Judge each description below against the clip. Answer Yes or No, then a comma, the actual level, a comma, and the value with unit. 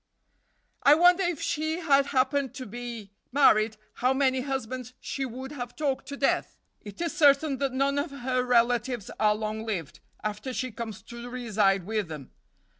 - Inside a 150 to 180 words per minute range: Yes, average, 170 wpm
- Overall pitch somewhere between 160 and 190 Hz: No, very high, 255 Hz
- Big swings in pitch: No, average, 4.1 semitones